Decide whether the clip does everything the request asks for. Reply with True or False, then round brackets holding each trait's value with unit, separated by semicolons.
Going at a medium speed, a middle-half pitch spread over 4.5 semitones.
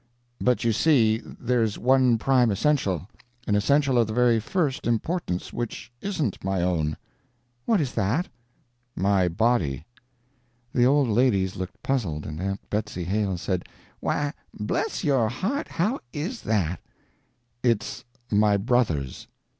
False (130 wpm; 5.6 semitones)